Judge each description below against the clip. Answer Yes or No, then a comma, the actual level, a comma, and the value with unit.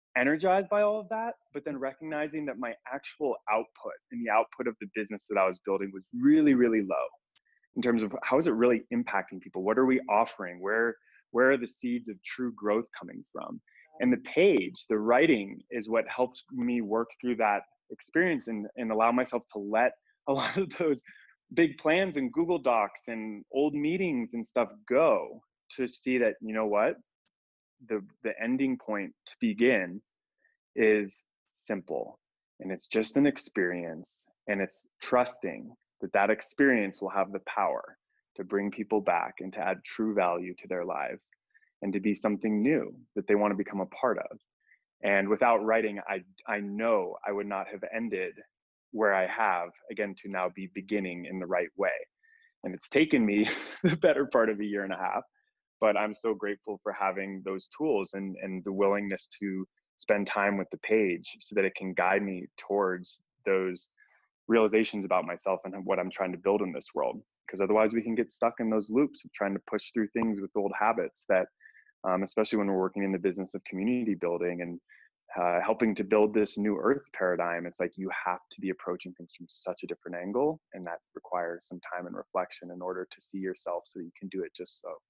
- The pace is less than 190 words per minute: No, average, 200 wpm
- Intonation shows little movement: No, average, 4.3 semitones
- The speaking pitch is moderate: No, low, 105 Hz